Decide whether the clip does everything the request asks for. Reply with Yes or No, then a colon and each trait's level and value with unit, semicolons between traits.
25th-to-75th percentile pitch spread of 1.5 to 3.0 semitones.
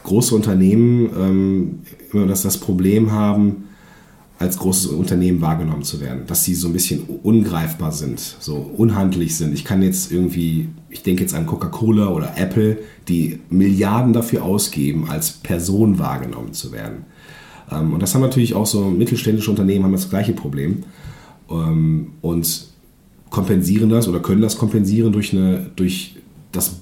No: average, 4.0 semitones